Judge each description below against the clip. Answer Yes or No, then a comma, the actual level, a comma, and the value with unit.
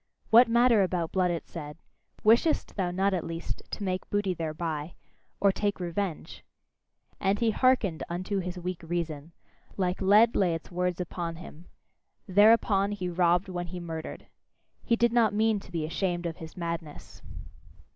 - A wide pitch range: No, average, 3.3 semitones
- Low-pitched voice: No, medium, 180 Hz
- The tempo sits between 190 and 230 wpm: No, average, 160 wpm